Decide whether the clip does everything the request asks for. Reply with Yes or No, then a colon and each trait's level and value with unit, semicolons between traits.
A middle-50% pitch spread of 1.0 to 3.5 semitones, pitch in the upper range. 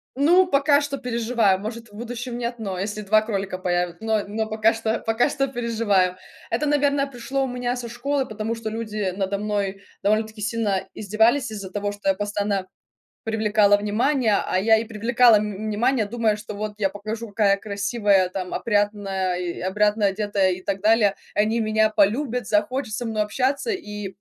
Yes: narrow, 2.6 semitones; high, 215 Hz